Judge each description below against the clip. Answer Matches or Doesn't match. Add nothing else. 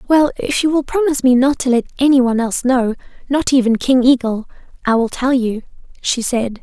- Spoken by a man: Doesn't match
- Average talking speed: Doesn't match